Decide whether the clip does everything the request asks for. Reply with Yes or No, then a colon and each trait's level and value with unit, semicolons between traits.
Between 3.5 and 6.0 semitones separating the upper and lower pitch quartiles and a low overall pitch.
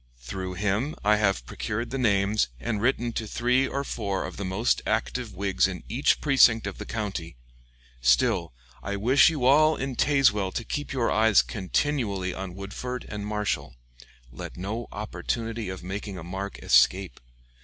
Yes: average, 4.2 semitones; low, 105 Hz